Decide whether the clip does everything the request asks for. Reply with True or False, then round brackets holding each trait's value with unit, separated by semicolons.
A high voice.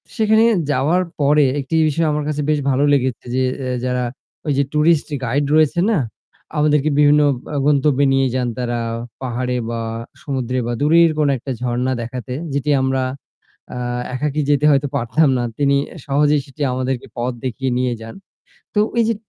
False (140 Hz)